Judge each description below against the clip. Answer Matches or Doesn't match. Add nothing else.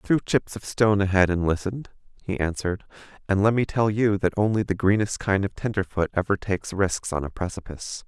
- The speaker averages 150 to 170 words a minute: Doesn't match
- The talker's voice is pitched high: Doesn't match